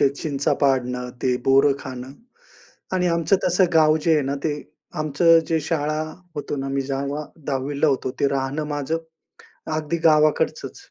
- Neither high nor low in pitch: Yes, medium, 145 Hz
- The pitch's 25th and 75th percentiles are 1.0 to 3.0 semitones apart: Yes, narrow, 2.5 semitones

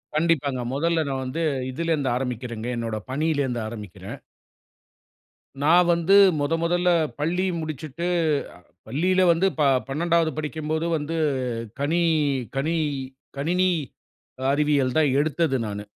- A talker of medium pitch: Yes, medium, 155 Hz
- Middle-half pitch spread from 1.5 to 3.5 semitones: No, average, 4.1 semitones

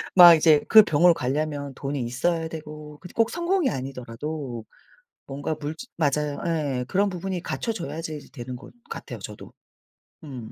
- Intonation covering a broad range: No, average, 4.1 semitones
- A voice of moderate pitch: Yes, medium, 150 Hz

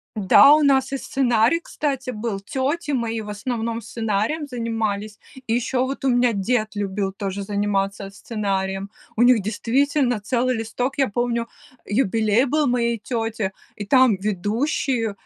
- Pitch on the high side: Yes, high, 230 Hz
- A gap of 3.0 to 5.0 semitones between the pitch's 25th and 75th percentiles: Yes, average, 3.8 semitones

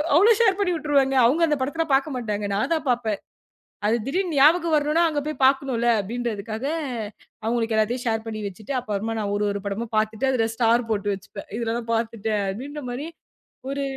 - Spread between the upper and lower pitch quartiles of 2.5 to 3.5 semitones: No, average, 5.0 semitones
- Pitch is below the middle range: No, high, 240 Hz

